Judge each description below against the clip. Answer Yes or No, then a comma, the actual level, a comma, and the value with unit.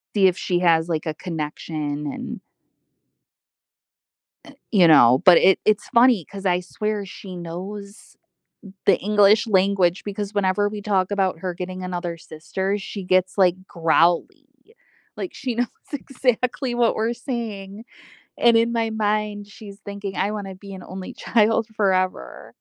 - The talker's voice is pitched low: No, high, 195 Hz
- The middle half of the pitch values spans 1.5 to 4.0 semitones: Yes, average, 2.9 semitones